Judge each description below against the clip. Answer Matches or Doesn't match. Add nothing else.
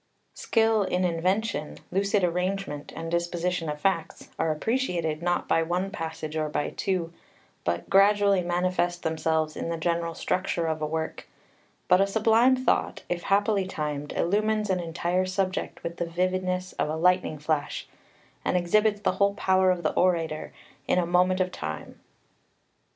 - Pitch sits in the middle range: Matches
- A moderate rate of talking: Matches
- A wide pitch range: Doesn't match